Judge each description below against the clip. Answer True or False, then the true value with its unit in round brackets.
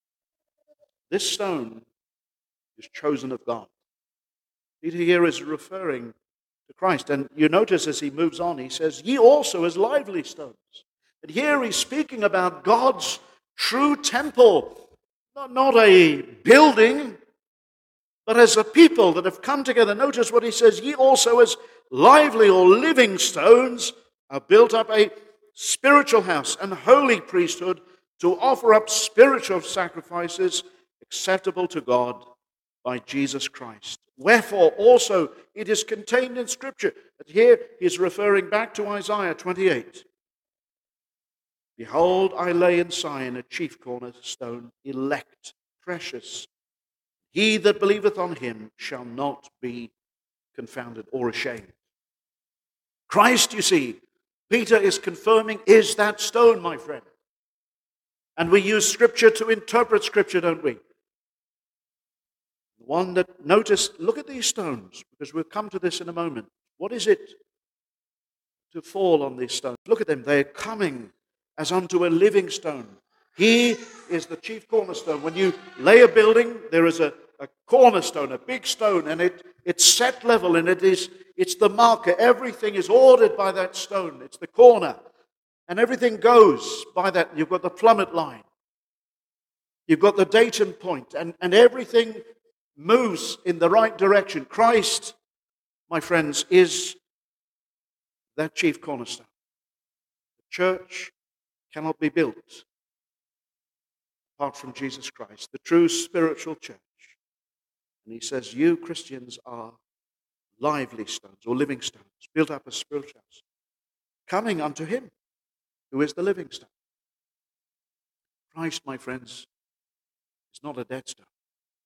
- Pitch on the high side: True (205 Hz)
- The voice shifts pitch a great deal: True (8.9 semitones)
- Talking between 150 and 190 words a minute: False (140 wpm)